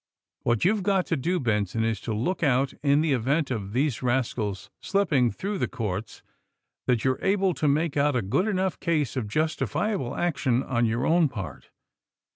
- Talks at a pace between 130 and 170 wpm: No, average, 185 wpm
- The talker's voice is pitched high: No, low, 135 Hz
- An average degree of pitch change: No, wide, 6.4 semitones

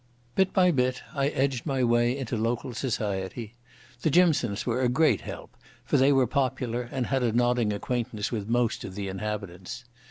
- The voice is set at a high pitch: No, low, 120 Hz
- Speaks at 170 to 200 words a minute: Yes, average, 180 wpm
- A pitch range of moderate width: Yes, average, 3.3 semitones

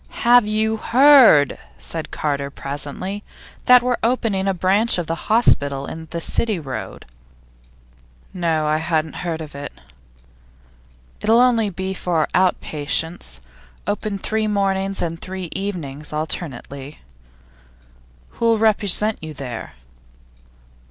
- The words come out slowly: Yes, slow, 120 wpm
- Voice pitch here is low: No, medium, 180 Hz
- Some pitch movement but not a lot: No, wide, 5.9 semitones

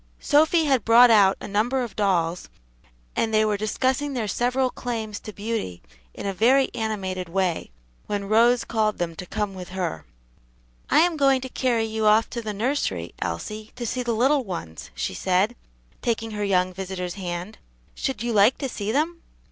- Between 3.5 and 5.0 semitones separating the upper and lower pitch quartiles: Yes, average, 4.4 semitones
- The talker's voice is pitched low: No, high, 215 Hz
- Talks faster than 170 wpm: Yes, average, 185 wpm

